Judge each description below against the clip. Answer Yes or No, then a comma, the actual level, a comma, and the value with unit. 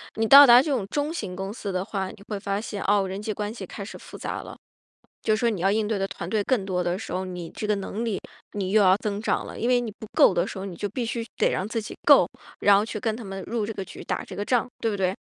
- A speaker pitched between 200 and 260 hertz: Yes, high, 205 Hz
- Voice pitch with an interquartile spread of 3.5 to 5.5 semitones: No, narrow, 2.6 semitones